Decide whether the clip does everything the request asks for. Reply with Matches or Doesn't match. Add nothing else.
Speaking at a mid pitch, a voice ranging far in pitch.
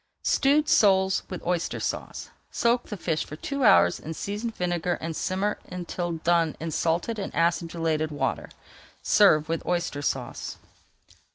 Doesn't match